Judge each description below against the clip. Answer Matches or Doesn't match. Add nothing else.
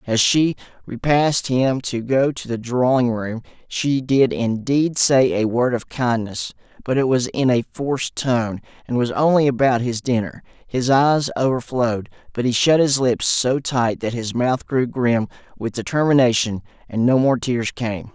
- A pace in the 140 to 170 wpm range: Doesn't match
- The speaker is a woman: Doesn't match